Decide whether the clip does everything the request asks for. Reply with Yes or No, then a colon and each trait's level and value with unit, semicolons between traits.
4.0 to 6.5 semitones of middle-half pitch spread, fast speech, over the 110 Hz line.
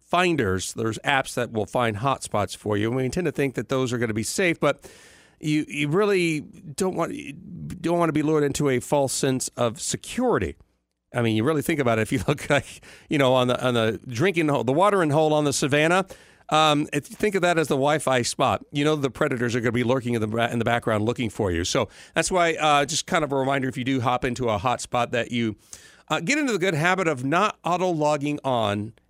Yes: average, 4.7 semitones; fast, 250 wpm; medium, 140 Hz